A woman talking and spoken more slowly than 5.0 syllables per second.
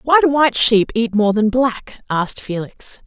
Yes: female; 4.5 syllables/s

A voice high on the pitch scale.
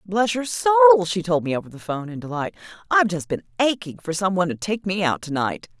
No: medium, 175 Hz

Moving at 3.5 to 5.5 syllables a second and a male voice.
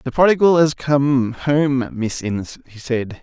Yes: 4.0 syllables/s; male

